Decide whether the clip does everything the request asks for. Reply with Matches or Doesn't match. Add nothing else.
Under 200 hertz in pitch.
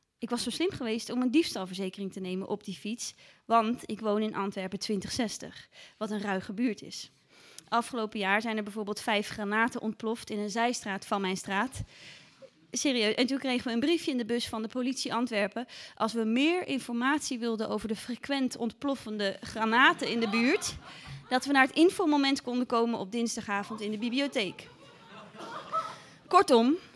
Doesn't match